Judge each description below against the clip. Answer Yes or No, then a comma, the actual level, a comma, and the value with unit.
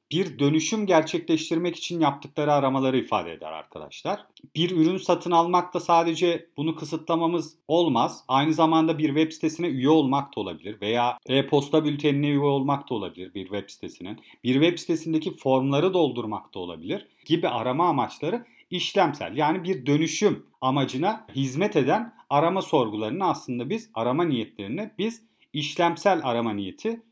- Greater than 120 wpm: Yes, fast, 140 wpm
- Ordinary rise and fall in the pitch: Yes, average, 3.9 semitones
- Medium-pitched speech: Yes, medium, 155 Hz